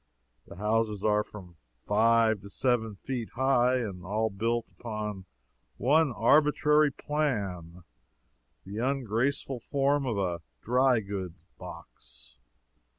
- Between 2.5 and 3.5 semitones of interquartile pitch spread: No, average, 4.6 semitones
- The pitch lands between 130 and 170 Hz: No, low, 110 Hz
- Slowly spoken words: Yes, slow, 110 wpm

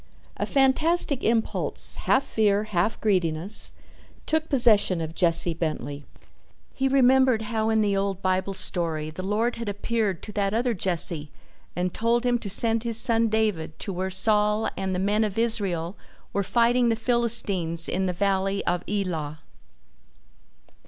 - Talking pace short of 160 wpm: Yes, average, 150 wpm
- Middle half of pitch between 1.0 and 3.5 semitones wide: No, average, 4.2 semitones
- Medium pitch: No, high, 205 Hz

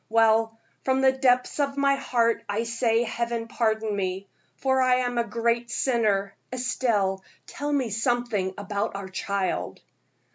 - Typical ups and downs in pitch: Yes, average, 3.4 semitones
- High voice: Yes, high, 230 Hz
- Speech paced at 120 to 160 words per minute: Yes, average, 145 wpm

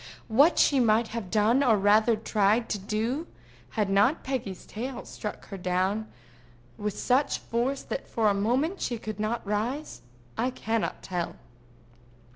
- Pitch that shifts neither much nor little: Yes, average, 3.2 semitones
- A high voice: Yes, high, 220 Hz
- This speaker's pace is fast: No, average, 150 wpm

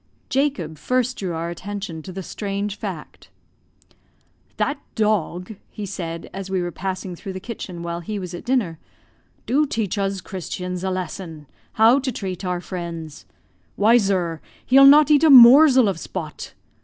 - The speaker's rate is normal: Yes, average, 160 wpm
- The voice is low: No, high, 195 Hz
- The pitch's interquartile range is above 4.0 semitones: Yes, average, 4.9 semitones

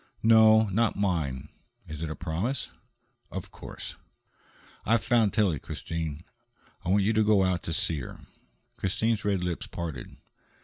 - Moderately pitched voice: No, very low, 95 Hz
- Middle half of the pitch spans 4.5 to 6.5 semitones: Yes, average, 5.0 semitones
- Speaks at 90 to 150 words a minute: Yes, average, 145 wpm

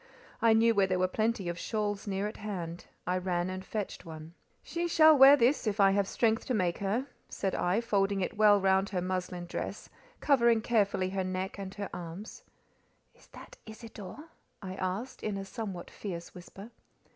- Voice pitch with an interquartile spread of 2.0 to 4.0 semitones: Yes, average, 3.1 semitones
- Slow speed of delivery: No, average, 185 wpm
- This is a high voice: Yes, high, 195 Hz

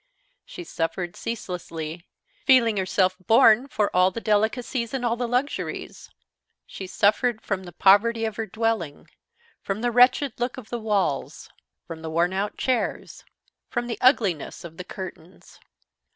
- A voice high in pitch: Yes, high, 215 Hz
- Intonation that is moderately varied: Yes, average, 4.6 semitones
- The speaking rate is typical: Yes, average, 150 wpm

